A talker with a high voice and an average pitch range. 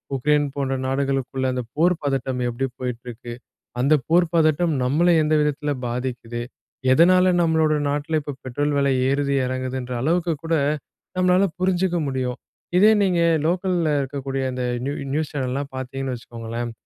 No: medium, 140 Hz; average, 3.9 semitones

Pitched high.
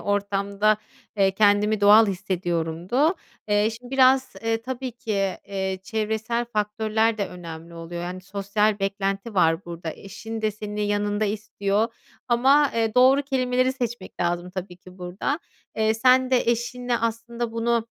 Yes: high, 215 Hz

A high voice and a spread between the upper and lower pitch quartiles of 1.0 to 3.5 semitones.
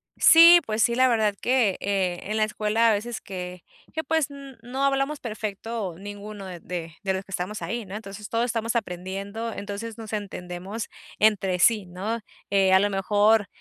Yes: high, 210 Hz; average, 3.1 semitones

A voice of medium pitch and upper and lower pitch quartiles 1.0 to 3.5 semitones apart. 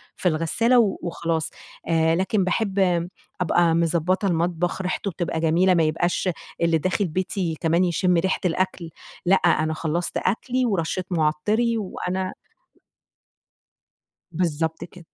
Yes: medium, 175 Hz; narrow, 2.4 semitones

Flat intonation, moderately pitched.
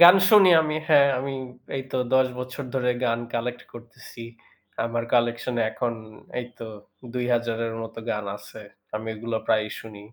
No: narrow, 2.3 semitones; low, 120 Hz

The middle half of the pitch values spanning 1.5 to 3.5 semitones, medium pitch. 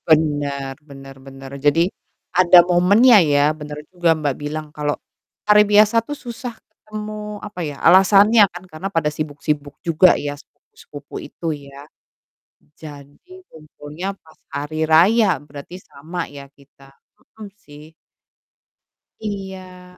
No: average, 5.3 semitones; medium, 160 Hz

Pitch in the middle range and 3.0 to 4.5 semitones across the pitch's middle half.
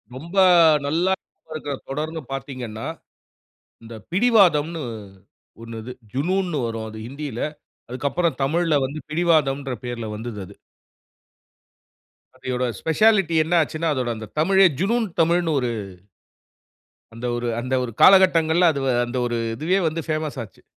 No: medium, 150 Hz; average, 5.3 semitones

